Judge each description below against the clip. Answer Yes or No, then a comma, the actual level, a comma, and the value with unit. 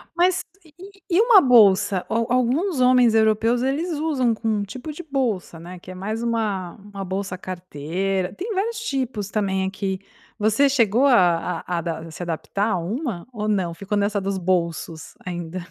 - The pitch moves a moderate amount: No, wide, 5.7 semitones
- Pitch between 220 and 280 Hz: No, high, 210 Hz